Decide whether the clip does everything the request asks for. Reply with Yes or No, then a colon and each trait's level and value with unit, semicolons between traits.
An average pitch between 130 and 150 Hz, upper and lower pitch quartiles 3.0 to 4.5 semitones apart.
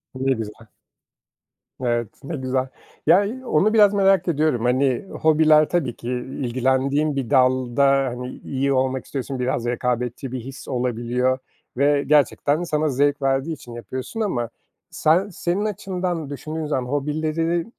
Yes: medium, 140 Hz; average, 3.8 semitones